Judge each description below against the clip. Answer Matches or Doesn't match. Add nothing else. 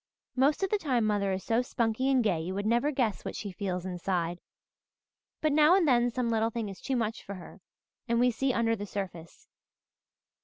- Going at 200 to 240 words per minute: Matches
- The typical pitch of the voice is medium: Doesn't match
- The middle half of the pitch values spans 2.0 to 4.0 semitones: Doesn't match